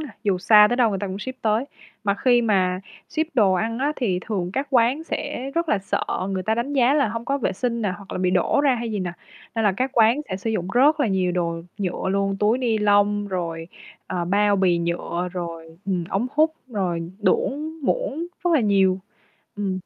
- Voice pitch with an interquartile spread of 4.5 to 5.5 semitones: Yes, average, 5.1 semitones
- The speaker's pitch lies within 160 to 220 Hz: Yes, high, 205 Hz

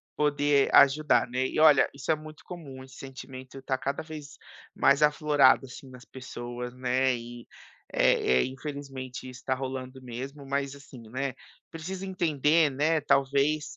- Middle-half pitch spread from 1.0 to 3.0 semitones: Yes, narrow, 2.4 semitones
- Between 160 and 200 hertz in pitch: No, medium, 140 Hz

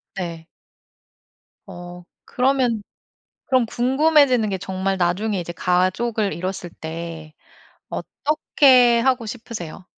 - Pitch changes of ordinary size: No, wide, 5.9 semitones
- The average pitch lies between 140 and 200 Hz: No, high, 210 Hz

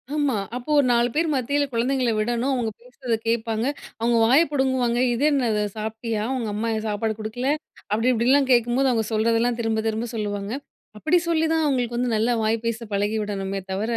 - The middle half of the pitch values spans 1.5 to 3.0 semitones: Yes, average, 2.7 semitones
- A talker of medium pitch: No, high, 235 Hz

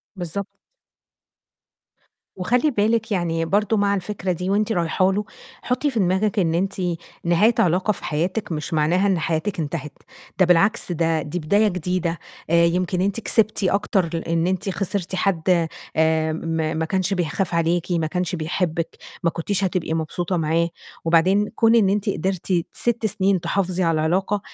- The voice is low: No, medium, 180 Hz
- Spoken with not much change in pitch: No, average, 3.4 semitones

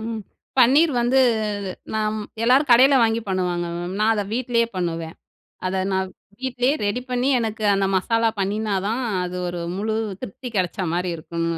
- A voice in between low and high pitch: No, high, 220 Hz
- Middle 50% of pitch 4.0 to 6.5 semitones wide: Yes, average, 4.6 semitones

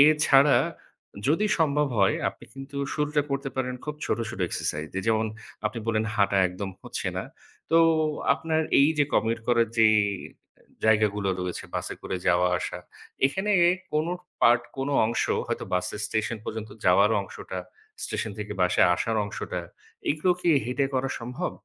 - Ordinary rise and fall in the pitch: No, wide, 5.9 semitones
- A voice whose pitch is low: Yes, low, 115 Hz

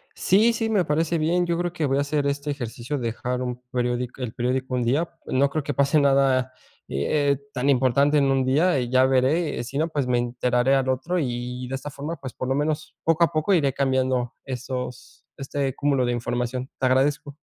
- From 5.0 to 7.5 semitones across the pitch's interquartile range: No, average, 2.8 semitones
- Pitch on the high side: No, low, 135 Hz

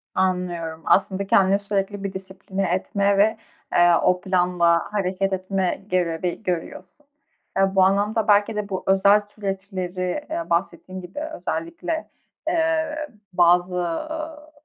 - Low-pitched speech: No, high, 195 Hz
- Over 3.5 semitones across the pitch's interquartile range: No, narrow, 2.5 semitones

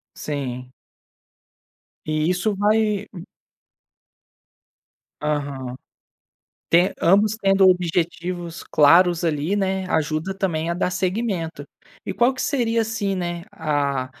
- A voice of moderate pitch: Yes, medium, 175 Hz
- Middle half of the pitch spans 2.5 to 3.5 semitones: No, average, 4.1 semitones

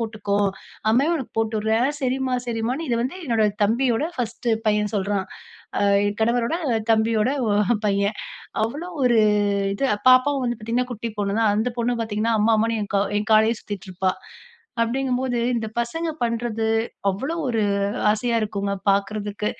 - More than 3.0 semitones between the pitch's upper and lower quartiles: No, average, 2.7 semitones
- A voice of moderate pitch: No, high, 225 Hz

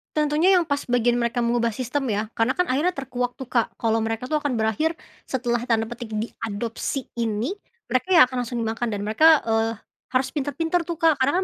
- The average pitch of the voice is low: No, high, 245 Hz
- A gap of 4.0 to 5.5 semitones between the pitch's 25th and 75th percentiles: Yes, average, 4.3 semitones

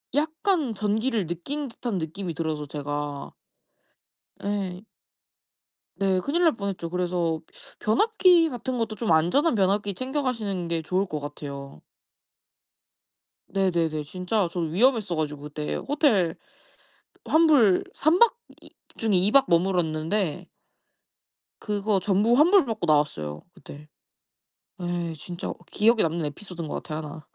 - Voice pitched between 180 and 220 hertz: Yes, high, 190 Hz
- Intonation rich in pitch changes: Yes, wide, 6.2 semitones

